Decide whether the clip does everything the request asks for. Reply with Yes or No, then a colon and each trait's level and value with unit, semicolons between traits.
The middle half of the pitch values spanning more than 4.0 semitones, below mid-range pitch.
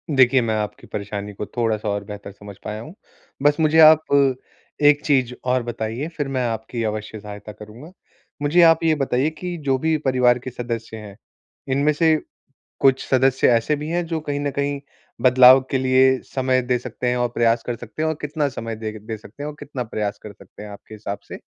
Yes: average, 4.8 semitones; low, 125 Hz